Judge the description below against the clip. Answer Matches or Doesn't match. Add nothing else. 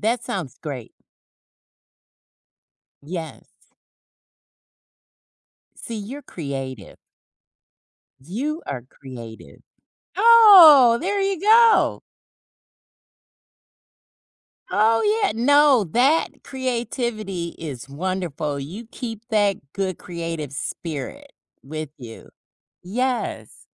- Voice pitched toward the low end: Doesn't match